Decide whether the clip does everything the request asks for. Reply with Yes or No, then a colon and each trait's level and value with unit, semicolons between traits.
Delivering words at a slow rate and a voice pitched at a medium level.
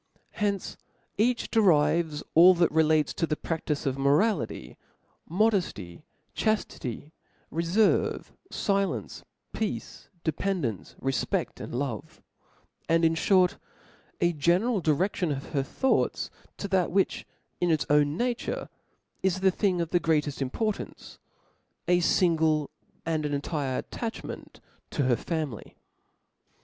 Yes: slow, 120 wpm; medium, 165 Hz